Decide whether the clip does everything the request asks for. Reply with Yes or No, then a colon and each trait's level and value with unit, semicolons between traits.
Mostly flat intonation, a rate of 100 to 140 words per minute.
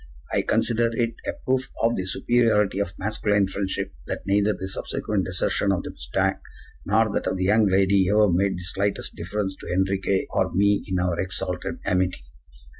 No: narrow, 2.0 semitones; average, 180 wpm